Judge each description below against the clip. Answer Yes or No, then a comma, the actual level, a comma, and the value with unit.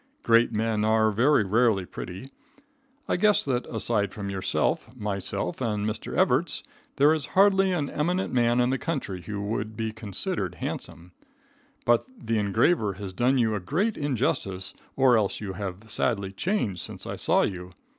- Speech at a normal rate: Yes, average, 165 wpm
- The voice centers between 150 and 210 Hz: No, low, 110 Hz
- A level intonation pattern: No, average, 4.9 semitones